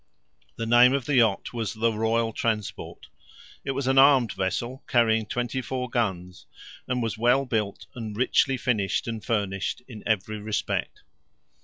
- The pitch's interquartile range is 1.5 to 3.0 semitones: Yes, average, 2.7 semitones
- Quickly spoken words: No, average, 155 wpm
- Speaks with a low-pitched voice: Yes, low, 115 Hz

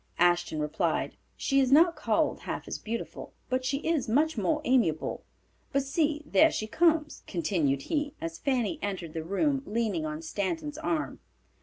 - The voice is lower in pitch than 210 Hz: No, very high, 255 Hz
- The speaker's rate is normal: Yes, average, 160 wpm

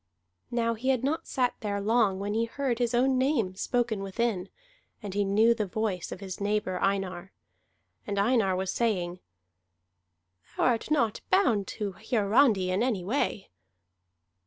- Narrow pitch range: No, average, 3.7 semitones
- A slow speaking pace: No, average, 155 wpm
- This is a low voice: No, high, 215 Hz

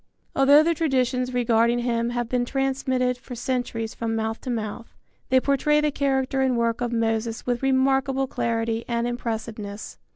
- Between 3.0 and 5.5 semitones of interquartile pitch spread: No, narrow, 2.5 semitones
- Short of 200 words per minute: Yes, average, 160 wpm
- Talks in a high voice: Yes, high, 245 Hz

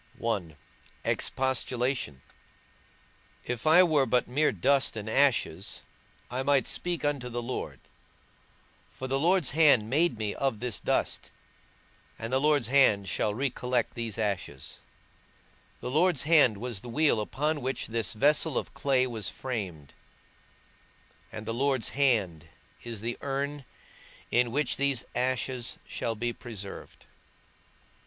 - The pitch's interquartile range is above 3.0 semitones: Yes, average, 3.9 semitones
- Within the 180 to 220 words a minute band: No, slow, 135 wpm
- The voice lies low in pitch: Yes, low, 125 Hz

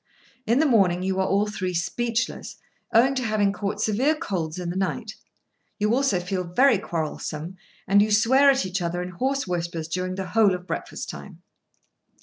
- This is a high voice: Yes, high, 195 Hz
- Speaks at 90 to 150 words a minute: No, average, 180 wpm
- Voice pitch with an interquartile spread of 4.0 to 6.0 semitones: Yes, average, 4.3 semitones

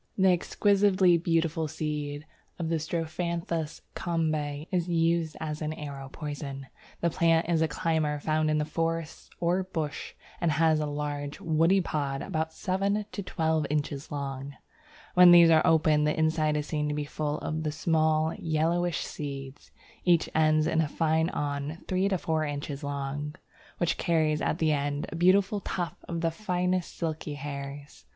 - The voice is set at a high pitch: No, medium, 160 Hz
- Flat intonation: Yes, narrow, 2.2 semitones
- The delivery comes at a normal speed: Yes, average, 160 wpm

